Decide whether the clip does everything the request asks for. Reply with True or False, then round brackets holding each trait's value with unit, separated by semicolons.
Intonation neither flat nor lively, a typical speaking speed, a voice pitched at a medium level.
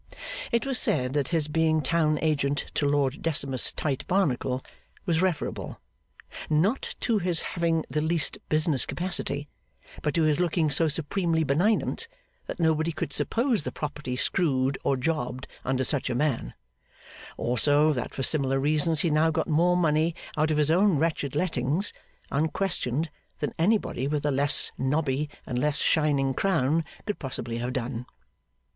True (3.4 semitones; 155 wpm; 150 Hz)